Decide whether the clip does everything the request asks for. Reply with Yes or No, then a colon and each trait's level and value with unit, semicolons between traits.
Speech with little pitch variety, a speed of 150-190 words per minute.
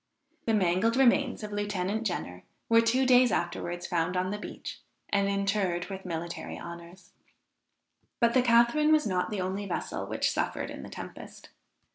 No: average, 4.2 semitones; average, 160 wpm